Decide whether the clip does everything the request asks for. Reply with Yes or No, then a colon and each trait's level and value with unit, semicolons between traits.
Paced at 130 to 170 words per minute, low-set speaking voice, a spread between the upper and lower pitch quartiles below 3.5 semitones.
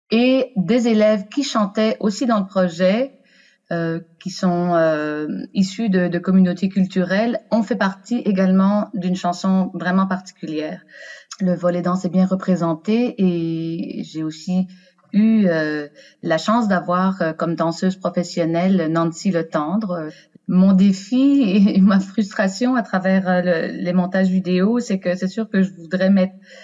No: average, 150 wpm; medium, 185 Hz; average, 3.0 semitones